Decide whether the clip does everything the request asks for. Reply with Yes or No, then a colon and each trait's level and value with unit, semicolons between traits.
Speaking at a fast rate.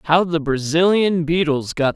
No: average, 155 wpm